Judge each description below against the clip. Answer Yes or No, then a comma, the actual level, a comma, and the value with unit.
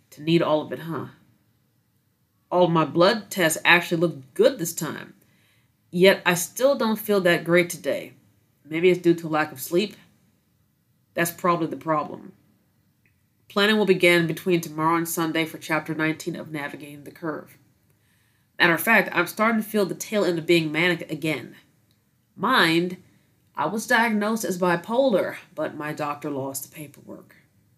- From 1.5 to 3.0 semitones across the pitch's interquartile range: Yes, average, 2.7 semitones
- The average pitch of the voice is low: No, medium, 170 Hz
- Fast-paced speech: No, average, 165 wpm